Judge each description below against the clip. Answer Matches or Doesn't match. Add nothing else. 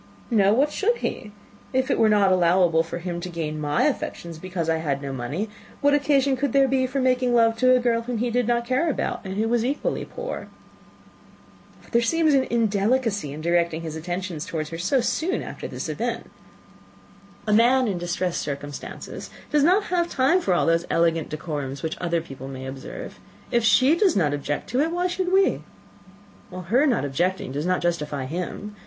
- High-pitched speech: Matches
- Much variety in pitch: Matches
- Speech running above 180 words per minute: Matches